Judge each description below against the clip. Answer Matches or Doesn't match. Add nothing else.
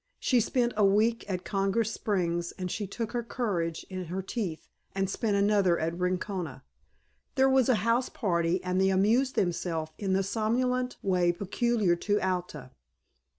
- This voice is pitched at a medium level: Doesn't match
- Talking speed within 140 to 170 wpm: Matches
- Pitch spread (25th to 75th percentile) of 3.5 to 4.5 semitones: Matches